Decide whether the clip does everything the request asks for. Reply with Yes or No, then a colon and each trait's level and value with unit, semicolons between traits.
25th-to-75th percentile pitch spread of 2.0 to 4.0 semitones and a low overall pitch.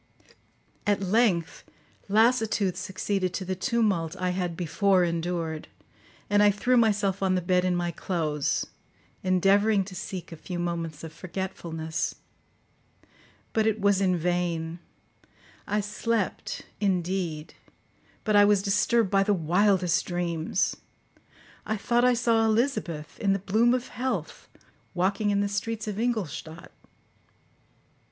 No: average, 3.3 semitones; high, 190 Hz